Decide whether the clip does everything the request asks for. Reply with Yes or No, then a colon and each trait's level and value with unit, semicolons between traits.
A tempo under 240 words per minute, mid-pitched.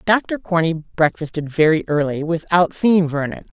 Yes: slow, 135 wpm; medium, 165 Hz